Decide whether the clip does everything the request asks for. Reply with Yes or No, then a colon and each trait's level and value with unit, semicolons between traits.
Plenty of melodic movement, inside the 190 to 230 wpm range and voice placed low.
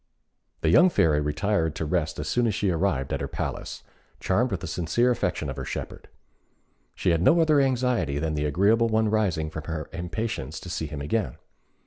Yes: wide, 6.4 semitones; average, 195 wpm; very low, 90 Hz